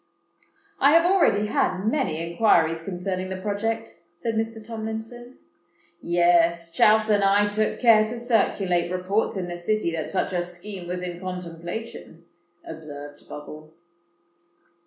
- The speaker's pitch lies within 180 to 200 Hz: Yes, medium, 185 Hz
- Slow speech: Yes, slow, 130 wpm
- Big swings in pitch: No, average, 4.3 semitones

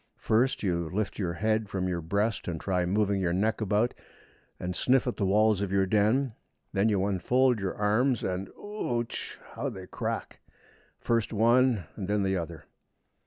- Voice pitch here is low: Yes, low, 105 Hz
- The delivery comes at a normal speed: Yes, average, 170 wpm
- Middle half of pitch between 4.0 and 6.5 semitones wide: No, average, 3.4 semitones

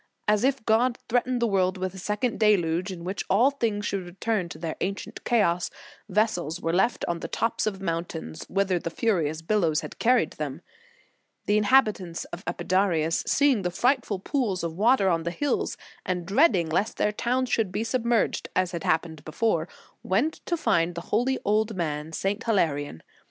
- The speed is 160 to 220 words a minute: Yes, average, 180 wpm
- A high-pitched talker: Yes, high, 195 Hz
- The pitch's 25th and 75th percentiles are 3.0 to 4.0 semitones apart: No, average, 4.9 semitones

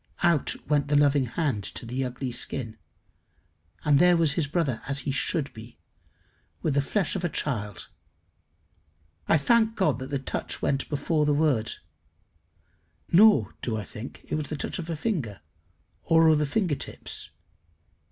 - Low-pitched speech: No, medium, 145 Hz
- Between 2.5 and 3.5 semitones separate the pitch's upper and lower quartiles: No, average, 4.1 semitones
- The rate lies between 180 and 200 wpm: No, average, 165 wpm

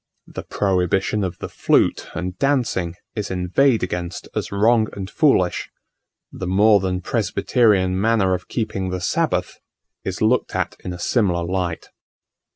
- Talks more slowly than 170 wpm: Yes, average, 145 wpm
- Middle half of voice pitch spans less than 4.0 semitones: Yes, average, 3.1 semitones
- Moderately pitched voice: No, very low, 95 Hz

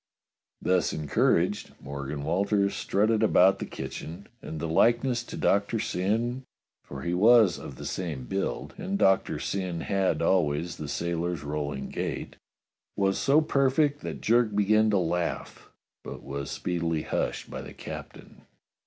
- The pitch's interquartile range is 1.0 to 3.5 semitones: No, average, 5.1 semitones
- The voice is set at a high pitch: No, very low, 95 Hz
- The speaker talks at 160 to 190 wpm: No, average, 145 wpm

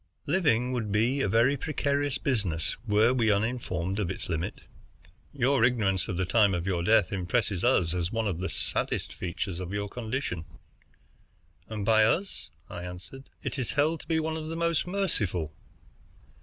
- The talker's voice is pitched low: Yes, low, 110 Hz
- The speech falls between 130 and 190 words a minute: Yes, average, 170 wpm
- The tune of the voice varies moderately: No, wide, 6.3 semitones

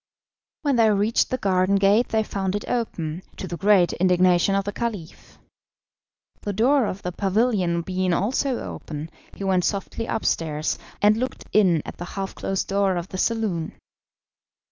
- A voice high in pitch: Yes, high, 195 Hz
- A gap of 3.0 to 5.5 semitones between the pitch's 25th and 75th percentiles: Yes, average, 3.4 semitones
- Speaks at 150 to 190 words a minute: Yes, average, 165 wpm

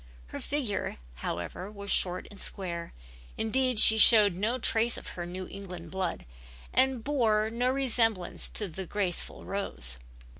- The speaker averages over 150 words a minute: No, average, 140 wpm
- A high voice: Yes, high, 205 Hz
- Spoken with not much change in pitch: No, average, 4.2 semitones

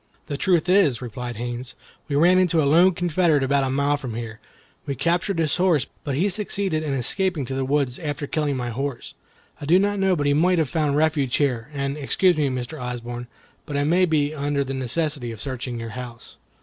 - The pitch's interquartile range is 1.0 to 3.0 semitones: No, average, 4.3 semitones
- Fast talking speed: Yes, fast, 215 wpm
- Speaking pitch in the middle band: Yes, medium, 145 Hz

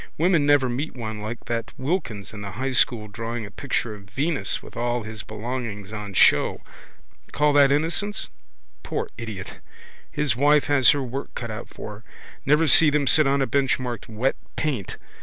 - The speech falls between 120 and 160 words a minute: No, average, 180 wpm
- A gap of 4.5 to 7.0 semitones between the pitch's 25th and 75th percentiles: Yes, average, 4.9 semitones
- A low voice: Yes, low, 125 Hz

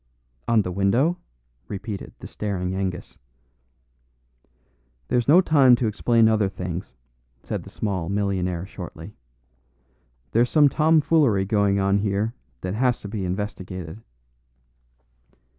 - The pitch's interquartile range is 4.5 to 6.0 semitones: No, average, 3.8 semitones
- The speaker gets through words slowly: Yes, slow, 115 wpm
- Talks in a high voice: No, low, 100 Hz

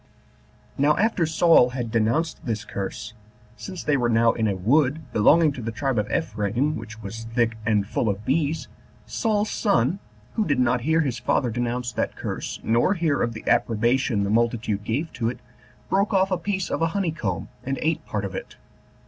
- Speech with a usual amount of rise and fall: No, wide, 6.2 semitones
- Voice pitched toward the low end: Yes, low, 125 Hz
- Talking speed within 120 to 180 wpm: No, average, 190 wpm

